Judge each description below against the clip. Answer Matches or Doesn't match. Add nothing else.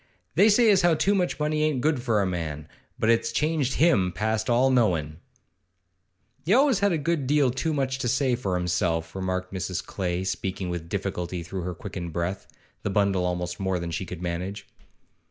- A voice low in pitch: Matches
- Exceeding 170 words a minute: Matches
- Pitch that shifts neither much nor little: Doesn't match